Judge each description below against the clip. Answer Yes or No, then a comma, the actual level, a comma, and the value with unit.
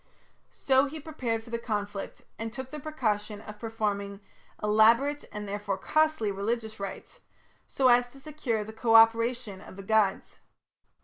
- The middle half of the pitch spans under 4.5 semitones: Yes, average, 3.7 semitones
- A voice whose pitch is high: Yes, high, 225 Hz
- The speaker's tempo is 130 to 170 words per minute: Yes, average, 150 wpm